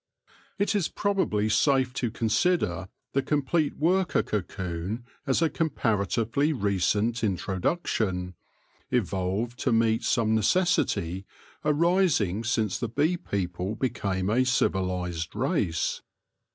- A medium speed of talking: No, slow, 105 wpm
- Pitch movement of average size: No, wide, 7.2 semitones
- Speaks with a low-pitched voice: Yes, low, 115 Hz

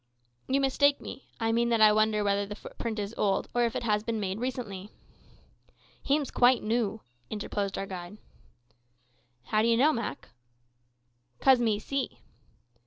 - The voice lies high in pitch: Yes, high, 220 Hz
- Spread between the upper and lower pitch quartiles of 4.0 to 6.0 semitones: No, average, 2.9 semitones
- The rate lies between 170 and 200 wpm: No, average, 155 wpm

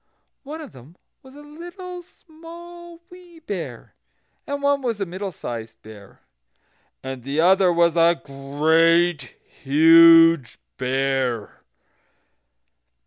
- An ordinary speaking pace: No, slow, 110 wpm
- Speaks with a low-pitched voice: No, medium, 170 Hz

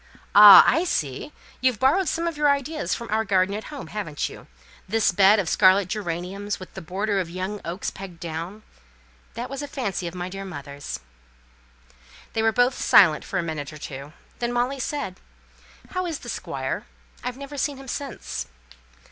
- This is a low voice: No, high, 205 Hz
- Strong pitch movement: Yes, wide, 6.5 semitones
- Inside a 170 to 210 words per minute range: Yes, average, 180 wpm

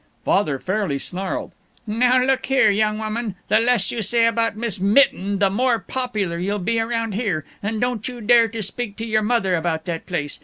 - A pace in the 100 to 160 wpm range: No, average, 195 wpm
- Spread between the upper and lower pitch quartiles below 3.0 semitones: No, average, 3.3 semitones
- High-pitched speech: Yes, high, 215 Hz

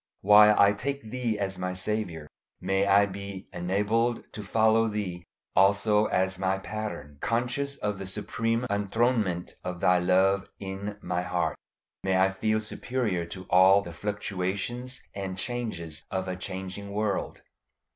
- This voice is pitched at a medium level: No, low, 100 Hz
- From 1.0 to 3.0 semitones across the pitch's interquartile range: Yes, narrow, 2.6 semitones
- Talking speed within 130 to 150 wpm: Yes, average, 145 wpm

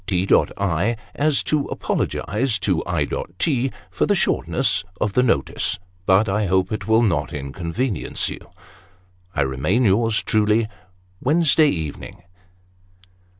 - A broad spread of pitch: No, average, 4.5 semitones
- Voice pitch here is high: No, low, 100 Hz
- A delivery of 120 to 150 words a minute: Yes, average, 140 wpm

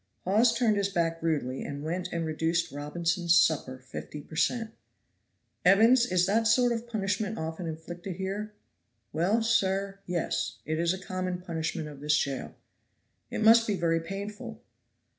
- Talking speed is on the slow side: No, average, 155 wpm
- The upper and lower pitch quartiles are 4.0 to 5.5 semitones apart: Yes, average, 4.6 semitones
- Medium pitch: Yes, medium, 180 Hz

